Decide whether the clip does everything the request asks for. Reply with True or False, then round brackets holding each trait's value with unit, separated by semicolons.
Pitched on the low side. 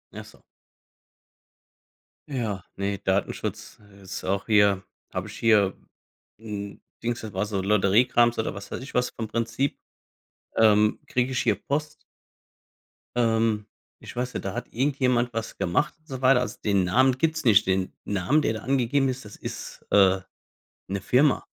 True (110 Hz)